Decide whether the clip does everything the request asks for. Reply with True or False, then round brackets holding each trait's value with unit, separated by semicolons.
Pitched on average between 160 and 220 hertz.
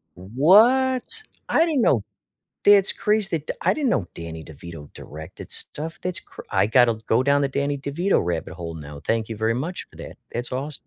False (135 Hz)